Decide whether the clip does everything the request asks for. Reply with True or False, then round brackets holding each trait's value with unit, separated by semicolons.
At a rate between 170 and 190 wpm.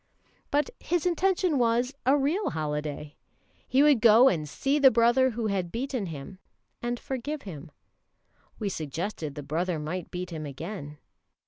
False (150 wpm)